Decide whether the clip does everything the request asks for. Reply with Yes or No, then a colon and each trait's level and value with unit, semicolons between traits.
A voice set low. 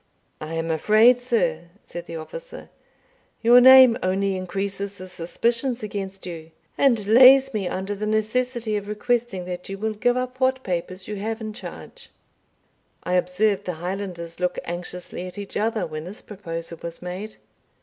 No: high, 200 Hz